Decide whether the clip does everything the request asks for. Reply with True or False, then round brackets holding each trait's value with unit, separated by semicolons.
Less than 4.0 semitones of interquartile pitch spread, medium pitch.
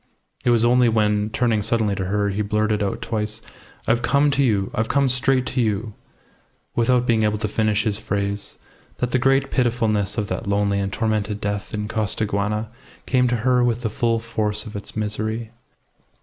False (2.5 semitones; 110 Hz)